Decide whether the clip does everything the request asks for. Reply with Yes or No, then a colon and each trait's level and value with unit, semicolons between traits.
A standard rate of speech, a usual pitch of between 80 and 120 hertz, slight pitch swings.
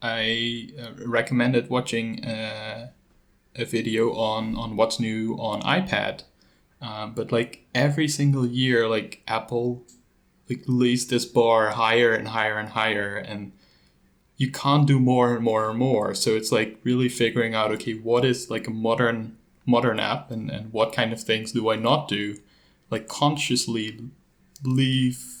Yes: average, 155 wpm; low, 115 Hz; narrow, 1.8 semitones